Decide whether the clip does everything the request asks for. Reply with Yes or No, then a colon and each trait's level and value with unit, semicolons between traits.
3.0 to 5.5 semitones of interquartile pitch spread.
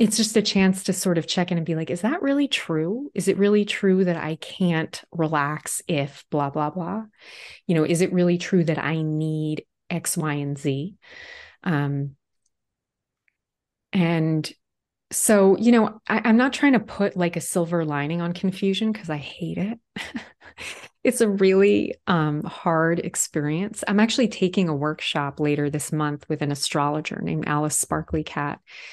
Yes: average, 4.6 semitones